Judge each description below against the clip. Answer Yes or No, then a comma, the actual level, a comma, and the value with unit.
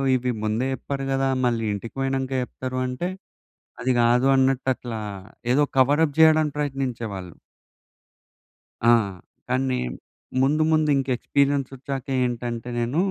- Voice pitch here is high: No, low, 130 Hz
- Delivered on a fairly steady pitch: Yes, narrow, 2.2 semitones